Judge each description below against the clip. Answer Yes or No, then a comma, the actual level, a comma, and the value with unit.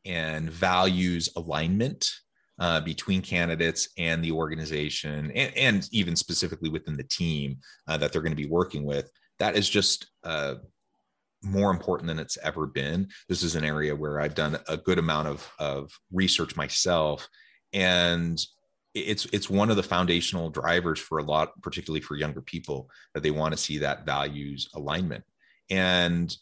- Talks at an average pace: Yes, average, 165 wpm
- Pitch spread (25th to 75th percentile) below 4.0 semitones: Yes, average, 3.1 semitones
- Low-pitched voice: Yes, very low, 80 Hz